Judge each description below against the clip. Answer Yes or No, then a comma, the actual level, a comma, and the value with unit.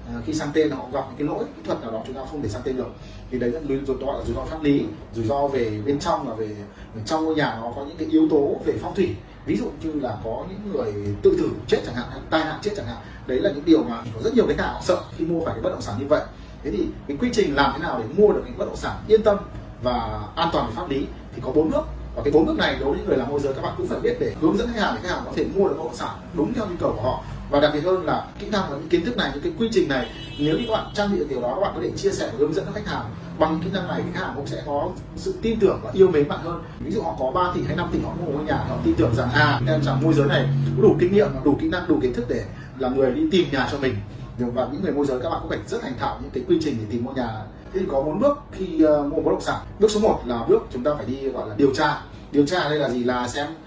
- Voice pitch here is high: No, medium, 145 Hz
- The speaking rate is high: Yes, fast, 335 wpm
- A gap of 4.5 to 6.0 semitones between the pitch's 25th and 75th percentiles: Yes, average, 5.2 semitones